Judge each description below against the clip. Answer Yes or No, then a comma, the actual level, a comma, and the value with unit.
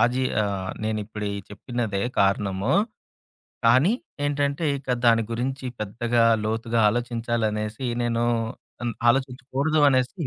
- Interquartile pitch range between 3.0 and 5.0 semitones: Yes, average, 3.3 semitones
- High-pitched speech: No, low, 120 Hz